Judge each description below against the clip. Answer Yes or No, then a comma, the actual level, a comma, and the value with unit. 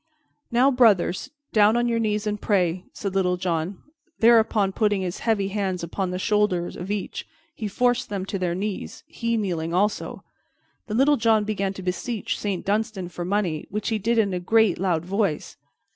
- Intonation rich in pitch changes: No, average, 3.3 semitones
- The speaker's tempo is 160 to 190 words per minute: Yes, average, 180 wpm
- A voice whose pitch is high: Yes, high, 205 Hz